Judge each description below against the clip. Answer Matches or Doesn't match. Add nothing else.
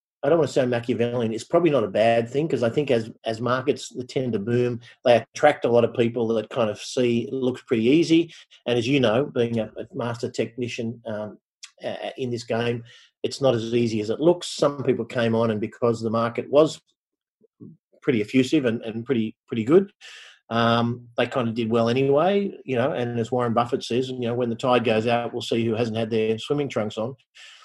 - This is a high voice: Doesn't match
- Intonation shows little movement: Matches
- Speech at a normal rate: Doesn't match